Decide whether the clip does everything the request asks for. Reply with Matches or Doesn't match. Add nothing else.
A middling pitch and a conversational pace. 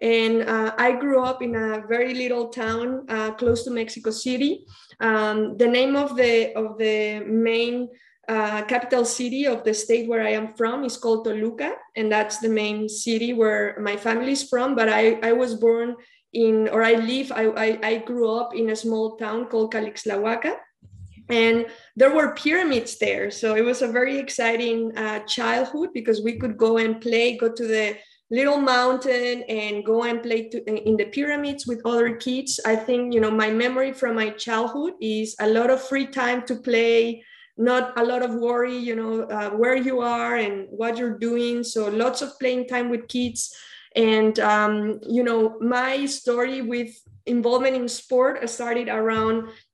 Doesn't match